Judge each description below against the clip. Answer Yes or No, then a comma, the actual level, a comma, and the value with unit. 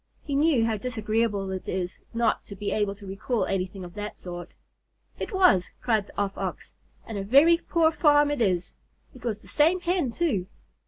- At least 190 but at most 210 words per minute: Yes, average, 195 wpm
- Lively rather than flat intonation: Yes, wide, 7.0 semitones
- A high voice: Yes, high, 220 Hz